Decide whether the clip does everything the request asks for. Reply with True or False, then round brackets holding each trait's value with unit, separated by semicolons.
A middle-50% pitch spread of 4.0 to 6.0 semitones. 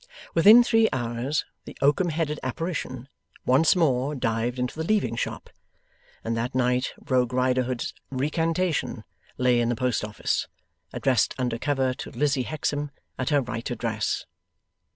False (3.6 semitones)